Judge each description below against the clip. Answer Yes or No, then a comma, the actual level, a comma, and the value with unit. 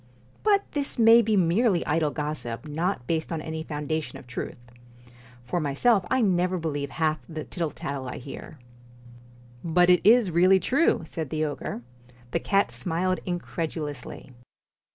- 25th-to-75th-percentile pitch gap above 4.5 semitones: No, average, 3.8 semitones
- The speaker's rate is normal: Yes, average, 155 wpm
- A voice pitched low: No, medium, 165 Hz